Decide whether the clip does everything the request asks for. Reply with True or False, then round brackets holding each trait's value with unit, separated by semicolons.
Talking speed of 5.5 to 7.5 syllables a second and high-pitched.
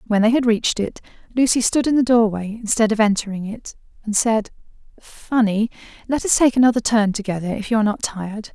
True (5.9 syllables/s; 220 Hz)